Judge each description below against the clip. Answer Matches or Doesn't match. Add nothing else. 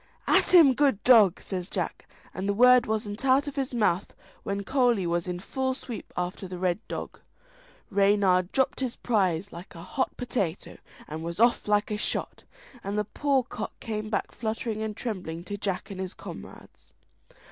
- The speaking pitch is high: Matches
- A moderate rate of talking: Matches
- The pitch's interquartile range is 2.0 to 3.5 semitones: Doesn't match